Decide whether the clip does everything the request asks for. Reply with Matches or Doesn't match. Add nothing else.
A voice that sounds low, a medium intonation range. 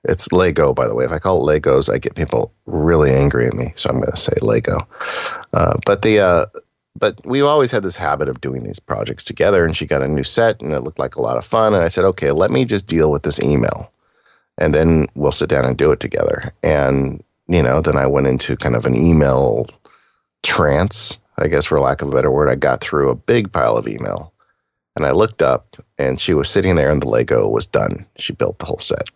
Doesn't match